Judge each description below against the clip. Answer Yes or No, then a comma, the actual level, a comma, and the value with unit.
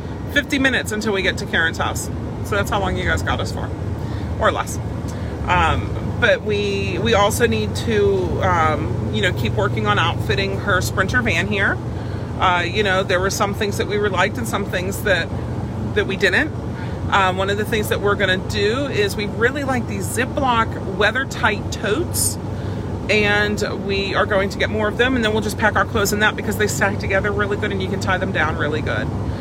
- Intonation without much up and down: Yes, narrow, 2.0 semitones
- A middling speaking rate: No, fast, 210 wpm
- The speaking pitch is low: Yes, low, 105 Hz